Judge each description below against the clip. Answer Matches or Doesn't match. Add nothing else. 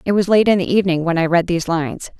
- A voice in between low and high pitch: Matches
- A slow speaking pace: Doesn't match